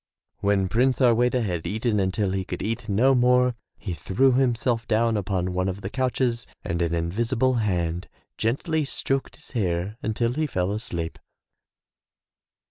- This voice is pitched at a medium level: No, low, 110 Hz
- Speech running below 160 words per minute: Yes, average, 150 wpm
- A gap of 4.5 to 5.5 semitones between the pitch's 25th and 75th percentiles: Yes, average, 4.8 semitones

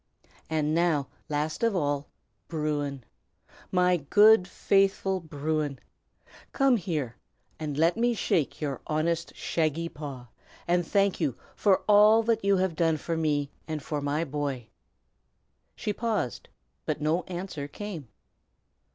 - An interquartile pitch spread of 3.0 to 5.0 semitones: Yes, average, 4.6 semitones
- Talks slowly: Yes, slow, 130 wpm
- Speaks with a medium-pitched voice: Yes, medium, 160 Hz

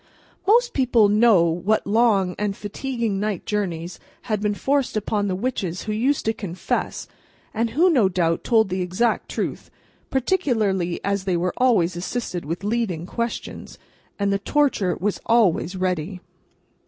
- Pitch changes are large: No, average, 4.3 semitones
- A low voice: No, high, 205 Hz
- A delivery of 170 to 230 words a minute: No, average, 145 wpm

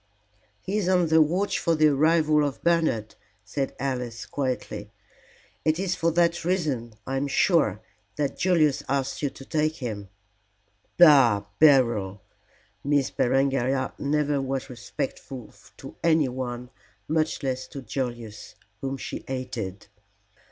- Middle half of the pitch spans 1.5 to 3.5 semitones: No, average, 4.0 semitones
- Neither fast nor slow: No, slow, 130 wpm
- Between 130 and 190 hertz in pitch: Yes, low, 135 Hz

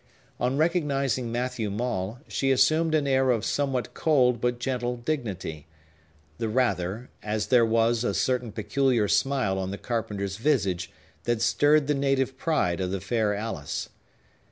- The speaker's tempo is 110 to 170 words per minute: Yes, average, 150 wpm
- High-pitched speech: No, low, 120 Hz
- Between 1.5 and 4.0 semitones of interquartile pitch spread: No, average, 4.5 semitones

